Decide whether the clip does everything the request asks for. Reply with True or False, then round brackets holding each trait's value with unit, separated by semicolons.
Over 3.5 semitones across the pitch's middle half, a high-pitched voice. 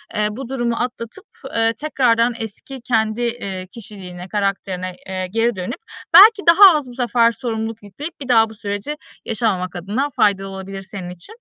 True (3.9 semitones; 225 Hz)